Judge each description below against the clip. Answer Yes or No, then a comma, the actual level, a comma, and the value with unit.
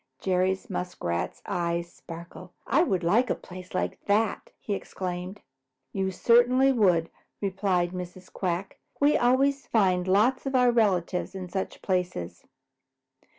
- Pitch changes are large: No, average, 4.3 semitones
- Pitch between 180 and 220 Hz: Yes, high, 190 Hz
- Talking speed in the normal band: No, slow, 130 wpm